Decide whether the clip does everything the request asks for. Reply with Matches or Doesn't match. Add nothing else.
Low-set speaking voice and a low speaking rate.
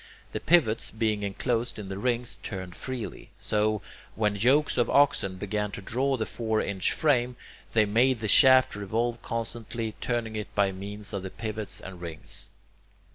Doesn't match